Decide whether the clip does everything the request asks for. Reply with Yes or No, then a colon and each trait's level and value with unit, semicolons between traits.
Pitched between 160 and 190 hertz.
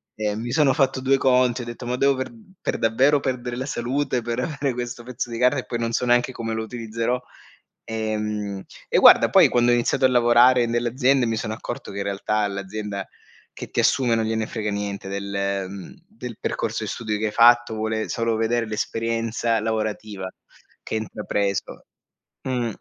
No: low, 115 Hz